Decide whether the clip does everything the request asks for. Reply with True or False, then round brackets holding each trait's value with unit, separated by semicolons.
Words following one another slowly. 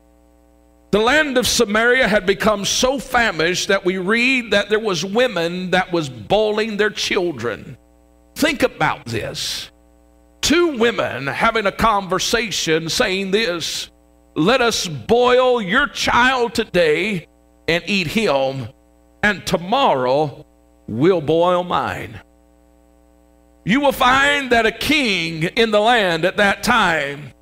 True (125 wpm)